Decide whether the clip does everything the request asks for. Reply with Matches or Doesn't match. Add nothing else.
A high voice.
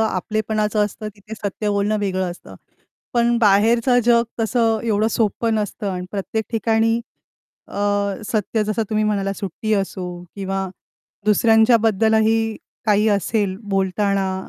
Matches